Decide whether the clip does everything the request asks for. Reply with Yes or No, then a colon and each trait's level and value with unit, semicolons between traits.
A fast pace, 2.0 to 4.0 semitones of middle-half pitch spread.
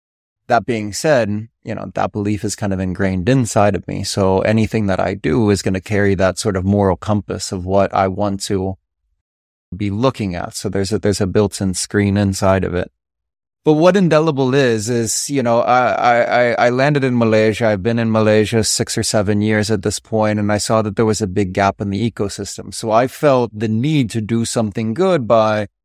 Yes: fast, 215 wpm; average, 2.8 semitones